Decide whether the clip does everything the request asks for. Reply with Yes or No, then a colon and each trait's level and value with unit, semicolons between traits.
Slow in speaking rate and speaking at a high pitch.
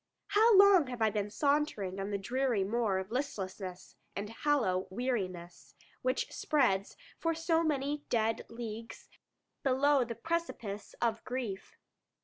Yes: slow, 130 wpm; high, 235 Hz